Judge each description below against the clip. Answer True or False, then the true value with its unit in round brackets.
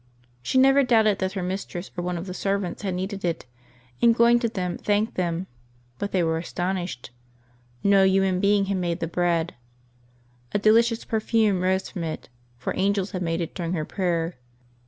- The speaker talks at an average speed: True (180 wpm)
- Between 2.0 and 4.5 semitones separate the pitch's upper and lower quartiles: True (2.7 semitones)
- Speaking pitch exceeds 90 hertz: True (190 Hz)